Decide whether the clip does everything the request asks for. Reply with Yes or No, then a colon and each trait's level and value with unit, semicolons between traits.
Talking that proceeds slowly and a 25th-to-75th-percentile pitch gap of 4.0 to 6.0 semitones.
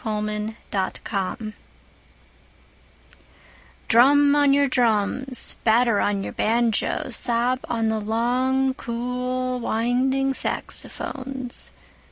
No: slow, 85 wpm; average, 2.9 semitones